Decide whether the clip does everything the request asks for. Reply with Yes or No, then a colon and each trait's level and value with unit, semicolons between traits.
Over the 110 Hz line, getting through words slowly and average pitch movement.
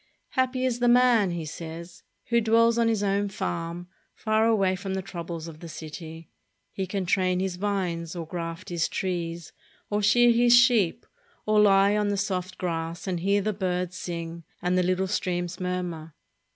No: medium, 185 Hz; average, 180 wpm; average, 3.6 semitones